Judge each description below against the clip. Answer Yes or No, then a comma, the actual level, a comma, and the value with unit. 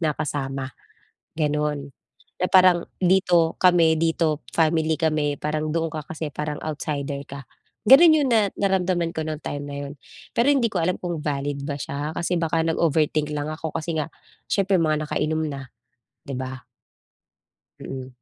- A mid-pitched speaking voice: Yes, medium, 155 Hz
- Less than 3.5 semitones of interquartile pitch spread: Yes, average, 2.7 semitones